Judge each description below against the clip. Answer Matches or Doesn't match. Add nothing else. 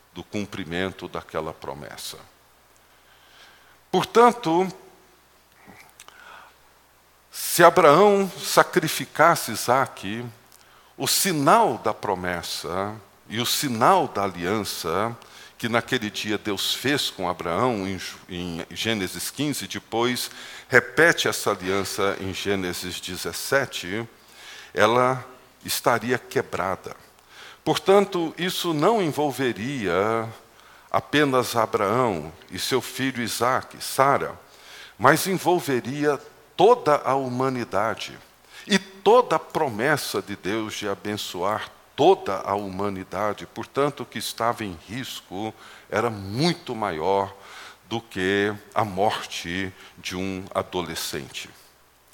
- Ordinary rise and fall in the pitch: Doesn't match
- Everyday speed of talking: Doesn't match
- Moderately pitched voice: Doesn't match